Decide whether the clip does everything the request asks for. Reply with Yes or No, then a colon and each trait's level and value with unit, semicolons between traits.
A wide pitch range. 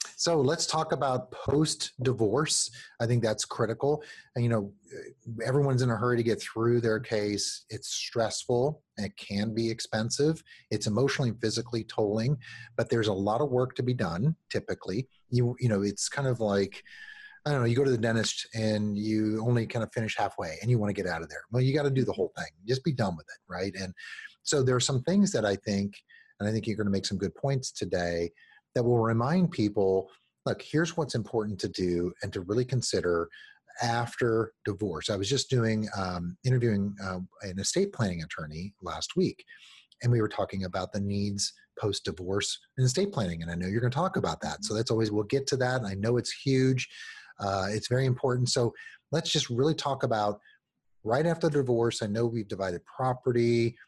No: average, 3.9 semitones